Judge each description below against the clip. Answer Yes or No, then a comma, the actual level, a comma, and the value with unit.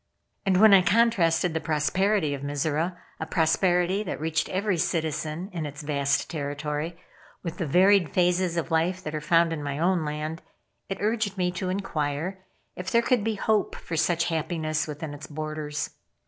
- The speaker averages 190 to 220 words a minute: No, average, 175 wpm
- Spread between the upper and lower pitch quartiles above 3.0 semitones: Yes, average, 3.4 semitones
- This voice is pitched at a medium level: Yes, medium, 165 Hz